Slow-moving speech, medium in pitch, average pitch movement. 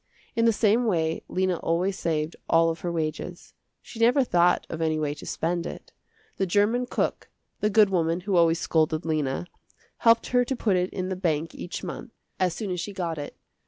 No: average, 200 wpm; medium, 175 Hz; average, 4.0 semitones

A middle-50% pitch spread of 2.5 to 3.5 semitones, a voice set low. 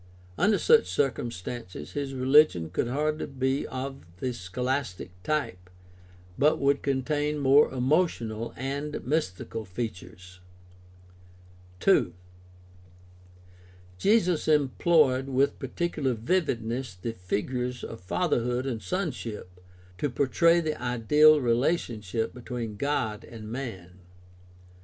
No: average, 4.8 semitones; low, 130 Hz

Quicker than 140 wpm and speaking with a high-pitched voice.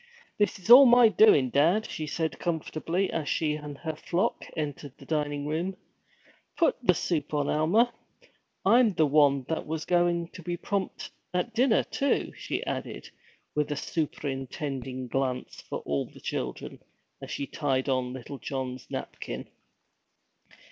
No: average, 150 wpm; medium, 155 Hz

